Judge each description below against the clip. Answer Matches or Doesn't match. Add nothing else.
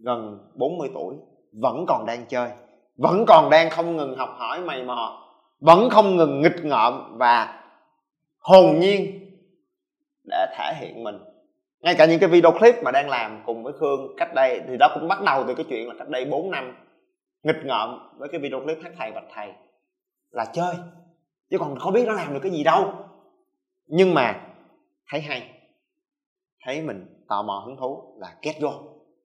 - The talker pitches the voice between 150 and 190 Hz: Matches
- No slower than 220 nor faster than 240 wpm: Doesn't match